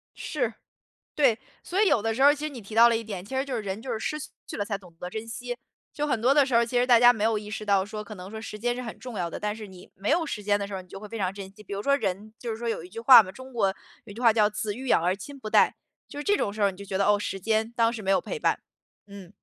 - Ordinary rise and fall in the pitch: Yes, average, 3.4 semitones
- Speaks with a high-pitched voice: Yes, high, 220 Hz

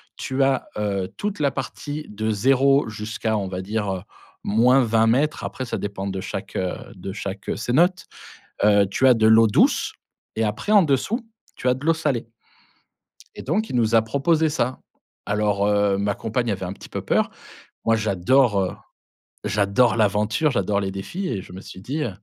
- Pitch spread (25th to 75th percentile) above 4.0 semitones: Yes, average, 5.0 semitones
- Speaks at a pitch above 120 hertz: No, low, 110 Hz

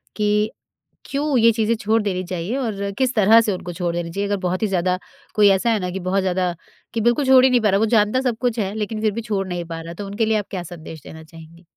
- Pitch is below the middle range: No, high, 205 Hz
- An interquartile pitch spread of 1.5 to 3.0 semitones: No, average, 3.6 semitones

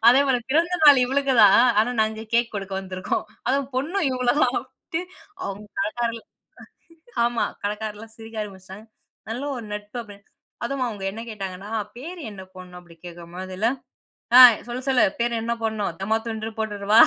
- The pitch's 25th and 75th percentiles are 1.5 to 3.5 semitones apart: No, average, 3.9 semitones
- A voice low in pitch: No, high, 220 Hz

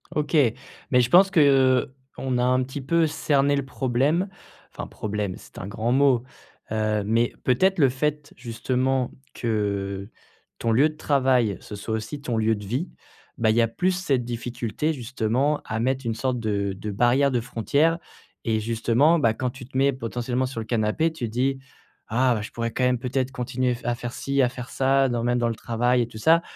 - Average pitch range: Yes, average, 3.0 semitones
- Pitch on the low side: Yes, low, 125 Hz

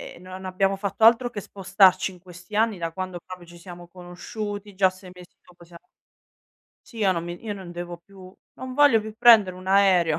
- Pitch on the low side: No, medium, 185 Hz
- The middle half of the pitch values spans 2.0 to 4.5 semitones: Yes, narrow, 2.6 semitones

